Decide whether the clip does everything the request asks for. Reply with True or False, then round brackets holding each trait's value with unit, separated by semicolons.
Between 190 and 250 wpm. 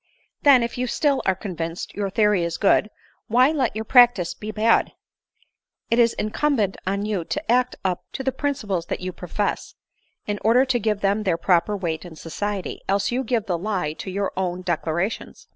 True (195 wpm)